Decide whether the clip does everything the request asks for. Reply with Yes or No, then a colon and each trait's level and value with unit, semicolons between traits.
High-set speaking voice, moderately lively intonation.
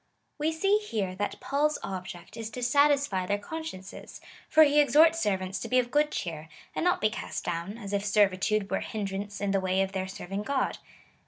No: high, 205 Hz; wide, 7.1 semitones